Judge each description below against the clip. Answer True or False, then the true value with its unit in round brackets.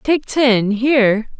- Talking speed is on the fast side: False (130 wpm)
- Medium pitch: False (245 Hz)